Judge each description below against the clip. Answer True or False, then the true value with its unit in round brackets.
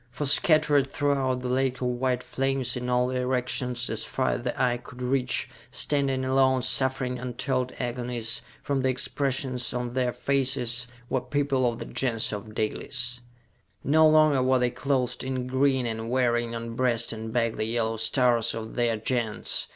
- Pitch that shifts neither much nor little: False (1.7 semitones)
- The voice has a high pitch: False (125 Hz)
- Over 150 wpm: True (165 wpm)